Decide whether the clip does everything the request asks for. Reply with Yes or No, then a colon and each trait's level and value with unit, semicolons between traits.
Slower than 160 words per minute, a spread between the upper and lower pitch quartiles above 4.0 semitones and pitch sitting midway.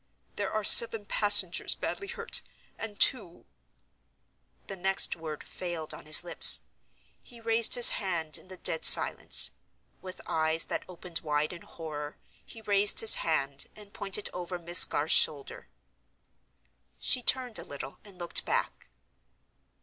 Yes: average, 140 wpm; average, 4.6 semitones; medium, 180 Hz